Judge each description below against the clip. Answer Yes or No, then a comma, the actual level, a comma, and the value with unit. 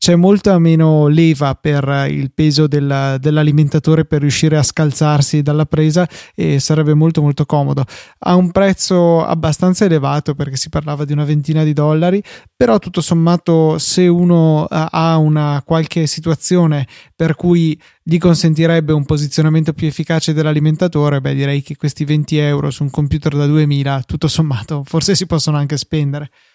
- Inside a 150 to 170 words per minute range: Yes, average, 155 wpm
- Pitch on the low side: No, medium, 155 Hz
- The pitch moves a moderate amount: No, narrow, 1.9 semitones